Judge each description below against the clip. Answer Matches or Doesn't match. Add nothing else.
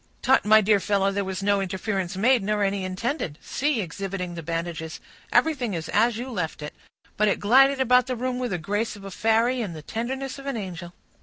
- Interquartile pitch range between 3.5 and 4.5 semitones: Doesn't match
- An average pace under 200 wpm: Doesn't match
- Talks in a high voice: Matches